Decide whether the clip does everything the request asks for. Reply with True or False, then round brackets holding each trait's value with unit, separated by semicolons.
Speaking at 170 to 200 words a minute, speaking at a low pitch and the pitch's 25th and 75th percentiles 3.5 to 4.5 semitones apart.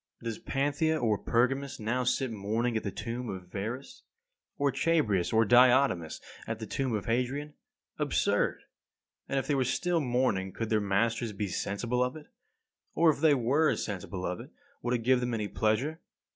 True (180 wpm; 120 Hz; 4.1 semitones)